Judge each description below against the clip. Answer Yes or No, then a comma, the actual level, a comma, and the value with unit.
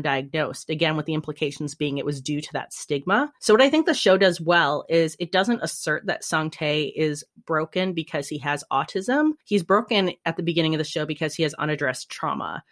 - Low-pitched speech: No, medium, 160 Hz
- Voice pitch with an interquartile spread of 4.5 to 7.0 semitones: No, average, 3.7 semitones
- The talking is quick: Yes, fast, 215 wpm